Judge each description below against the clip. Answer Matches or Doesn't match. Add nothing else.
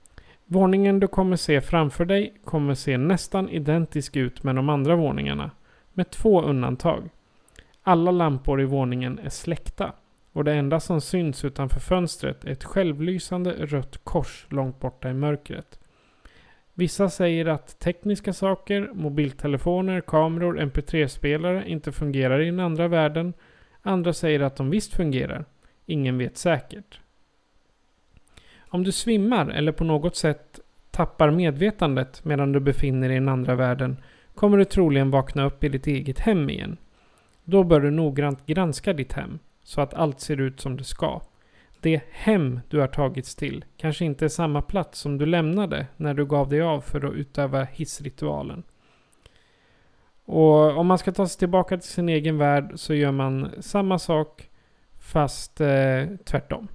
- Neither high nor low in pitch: Matches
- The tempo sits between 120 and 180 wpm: Matches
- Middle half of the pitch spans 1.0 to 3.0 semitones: Doesn't match